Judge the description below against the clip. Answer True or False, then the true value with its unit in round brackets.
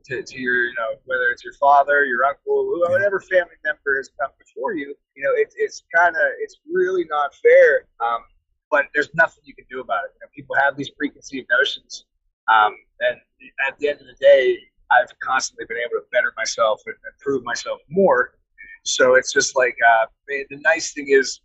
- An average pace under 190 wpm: False (200 wpm)